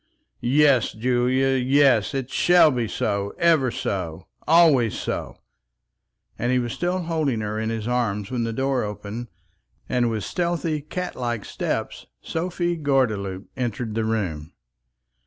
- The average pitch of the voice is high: No, low, 125 Hz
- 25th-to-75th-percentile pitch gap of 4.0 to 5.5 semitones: Yes, average, 4.9 semitones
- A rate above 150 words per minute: No, average, 140 wpm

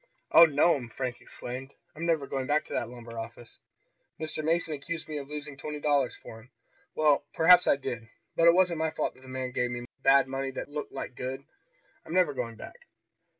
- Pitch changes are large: No, average, 3.9 semitones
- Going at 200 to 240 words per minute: Yes, fast, 205 wpm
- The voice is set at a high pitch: No, medium, 140 Hz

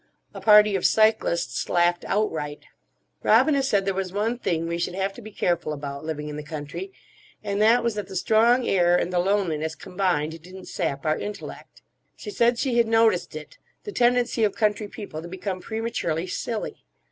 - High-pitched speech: Yes, high, 195 Hz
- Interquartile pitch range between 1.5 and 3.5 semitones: No, average, 4.6 semitones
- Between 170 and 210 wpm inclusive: Yes, average, 180 wpm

